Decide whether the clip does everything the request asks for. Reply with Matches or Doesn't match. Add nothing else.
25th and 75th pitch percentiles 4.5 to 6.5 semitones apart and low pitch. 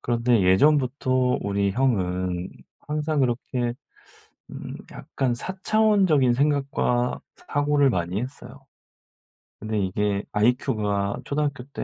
Matches